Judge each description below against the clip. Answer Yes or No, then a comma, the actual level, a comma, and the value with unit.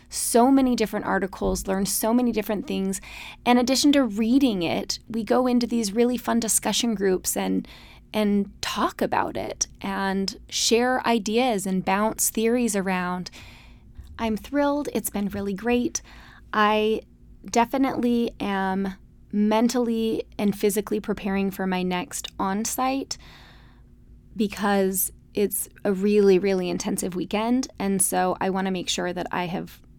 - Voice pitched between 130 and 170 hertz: No, high, 210 Hz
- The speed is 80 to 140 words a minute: Yes, slow, 135 wpm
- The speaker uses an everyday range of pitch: Yes, average, 3.5 semitones